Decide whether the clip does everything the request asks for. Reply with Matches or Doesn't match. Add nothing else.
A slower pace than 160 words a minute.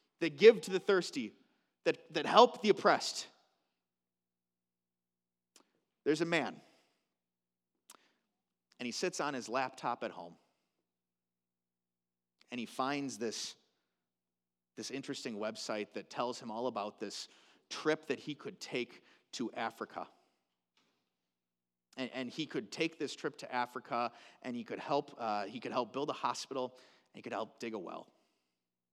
Matches